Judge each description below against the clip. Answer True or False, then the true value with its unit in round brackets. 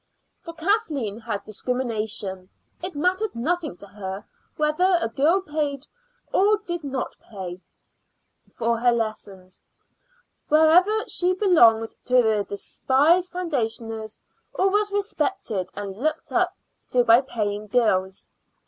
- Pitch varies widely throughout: True (8.4 semitones)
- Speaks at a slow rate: True (120 wpm)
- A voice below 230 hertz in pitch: False (250 Hz)